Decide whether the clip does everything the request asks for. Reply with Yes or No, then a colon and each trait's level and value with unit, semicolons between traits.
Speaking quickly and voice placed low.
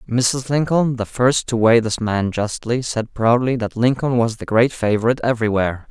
No: average, 185 wpm; low, 120 Hz